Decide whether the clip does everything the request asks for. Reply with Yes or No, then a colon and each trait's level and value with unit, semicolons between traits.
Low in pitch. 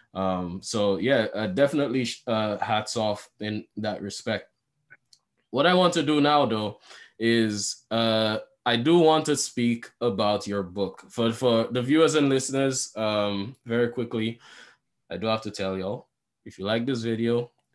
Yes: low, 115 Hz